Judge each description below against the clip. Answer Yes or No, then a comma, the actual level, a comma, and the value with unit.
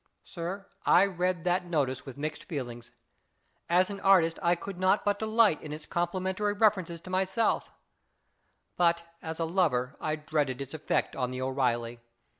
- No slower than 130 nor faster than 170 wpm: Yes, average, 160 wpm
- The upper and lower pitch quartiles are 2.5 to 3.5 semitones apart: No, average, 4.7 semitones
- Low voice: No, medium, 170 Hz